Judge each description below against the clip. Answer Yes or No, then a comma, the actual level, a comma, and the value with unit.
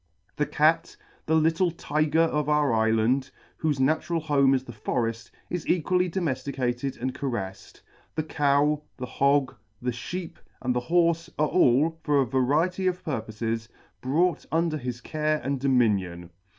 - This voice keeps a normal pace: Yes, average, 150 wpm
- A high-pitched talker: No, medium, 140 Hz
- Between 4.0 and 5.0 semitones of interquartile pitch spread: Yes, average, 4.3 semitones